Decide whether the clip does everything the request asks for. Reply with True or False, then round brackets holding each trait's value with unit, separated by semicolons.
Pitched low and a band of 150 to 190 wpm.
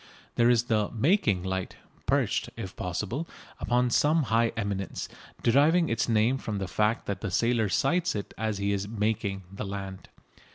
True (110 Hz; 165 wpm)